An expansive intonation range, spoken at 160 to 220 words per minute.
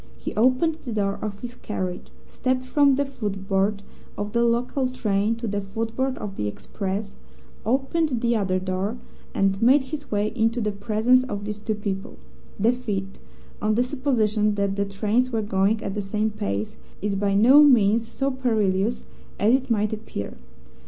No: average, 3.8 semitones; average, 170 wpm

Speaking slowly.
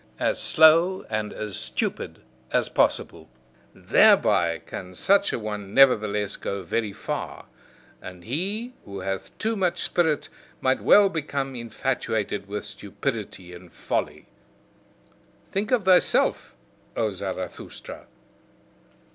Yes: slow, 115 wpm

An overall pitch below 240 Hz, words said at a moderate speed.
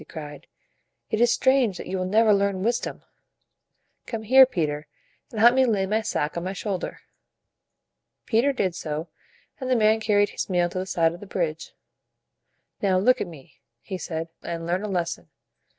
Yes: high, 190 Hz; average, 185 wpm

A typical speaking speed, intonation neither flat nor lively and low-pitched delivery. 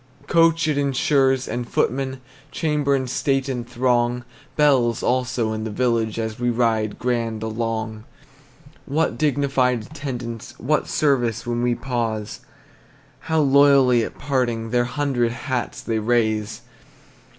No: slow, 130 wpm; average, 3.0 semitones; low, 125 Hz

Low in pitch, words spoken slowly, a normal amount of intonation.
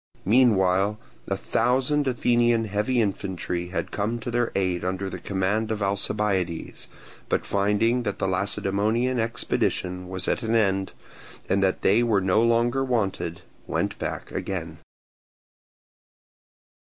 Yes: low, 100 Hz; slow, 130 wpm; average, 3.8 semitones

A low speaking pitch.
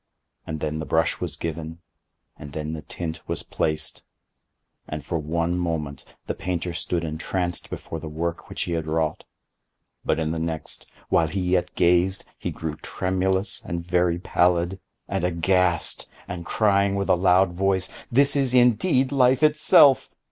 Yes: very low, 85 Hz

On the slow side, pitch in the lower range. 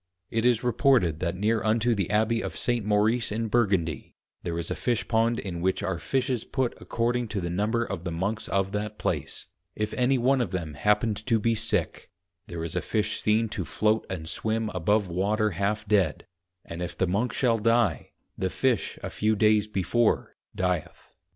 No: average, 190 wpm; low, 105 Hz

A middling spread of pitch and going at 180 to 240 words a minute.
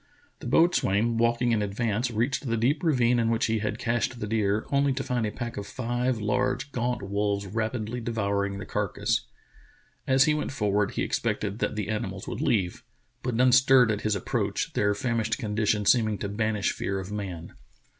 Yes: average, 3.0 semitones; average, 190 wpm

